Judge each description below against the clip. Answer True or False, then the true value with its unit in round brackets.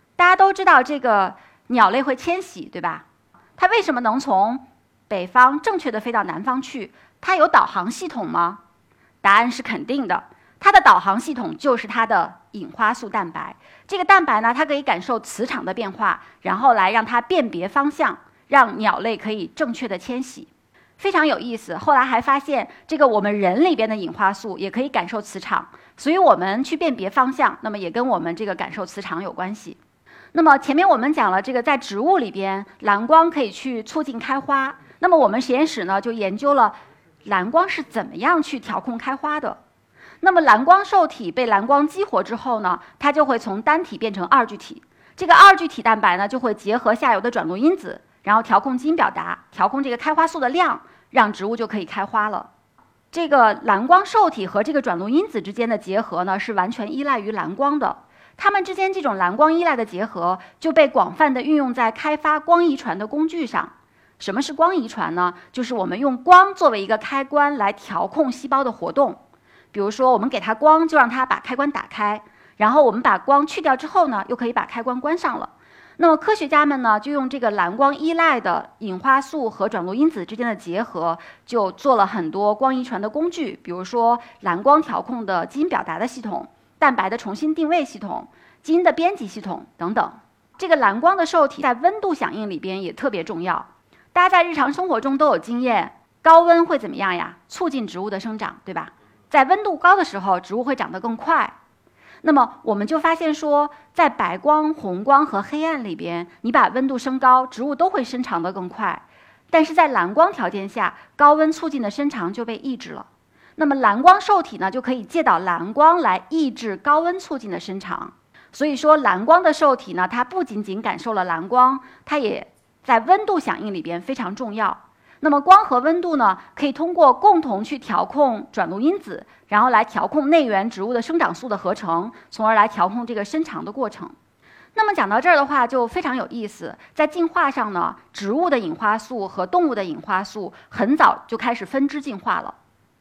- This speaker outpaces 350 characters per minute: False (300 characters per minute)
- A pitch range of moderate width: False (6.6 semitones)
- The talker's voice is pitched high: True (260 Hz)